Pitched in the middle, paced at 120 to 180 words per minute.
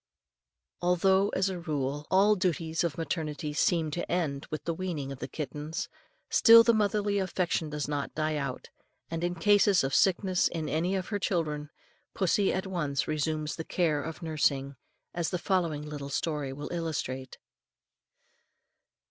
Yes: medium, 165 Hz; average, 160 wpm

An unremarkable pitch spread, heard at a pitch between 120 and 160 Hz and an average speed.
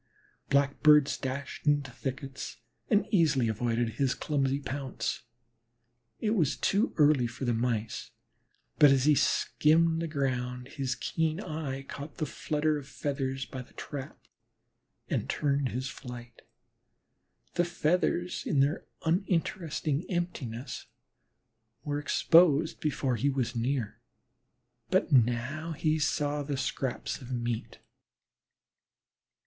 No: average, 3.2 semitones; medium, 140 Hz; slow, 120 wpm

